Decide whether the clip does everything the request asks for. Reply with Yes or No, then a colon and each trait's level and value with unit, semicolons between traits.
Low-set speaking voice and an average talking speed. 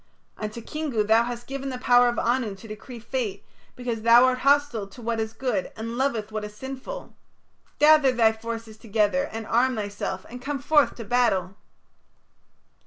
No: high, 235 Hz; average, 175 wpm